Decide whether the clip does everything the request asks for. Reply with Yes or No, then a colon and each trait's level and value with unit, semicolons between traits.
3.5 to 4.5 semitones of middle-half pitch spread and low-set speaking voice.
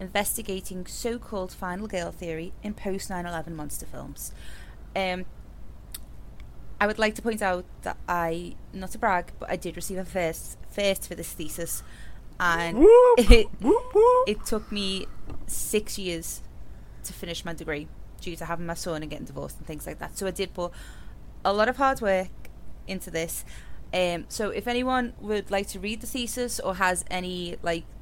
No: average, 3.8 semitones; high, 190 Hz